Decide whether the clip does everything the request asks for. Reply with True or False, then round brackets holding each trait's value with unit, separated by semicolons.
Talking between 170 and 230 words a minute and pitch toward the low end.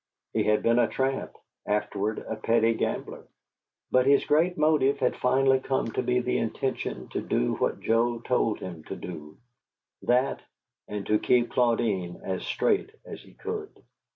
False (160 wpm; 120 Hz)